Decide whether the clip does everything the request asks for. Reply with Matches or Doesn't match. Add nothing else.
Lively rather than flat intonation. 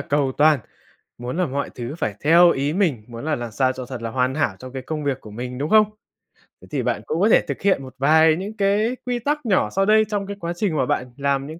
Matches